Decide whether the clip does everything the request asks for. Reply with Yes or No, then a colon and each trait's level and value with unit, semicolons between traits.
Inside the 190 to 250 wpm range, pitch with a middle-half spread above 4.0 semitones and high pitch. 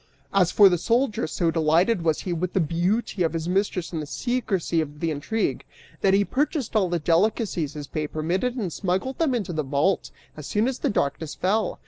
No: average, 200 wpm; average, 5.1 semitones; medium, 180 Hz